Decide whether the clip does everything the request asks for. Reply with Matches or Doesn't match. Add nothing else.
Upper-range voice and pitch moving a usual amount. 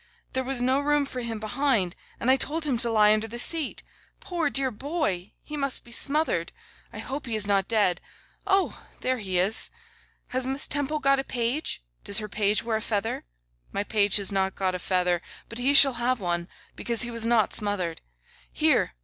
Matches